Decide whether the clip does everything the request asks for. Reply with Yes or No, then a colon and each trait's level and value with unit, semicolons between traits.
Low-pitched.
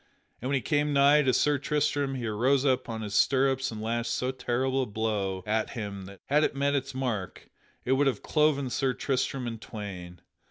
Yes: low, 130 Hz